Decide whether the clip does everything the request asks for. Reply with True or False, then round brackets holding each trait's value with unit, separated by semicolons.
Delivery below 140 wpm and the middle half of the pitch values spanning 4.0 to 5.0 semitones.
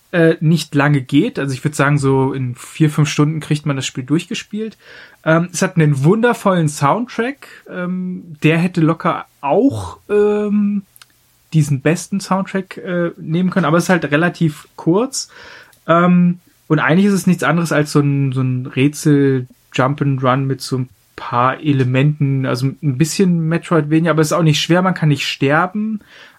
False (160 wpm; 4.3 semitones)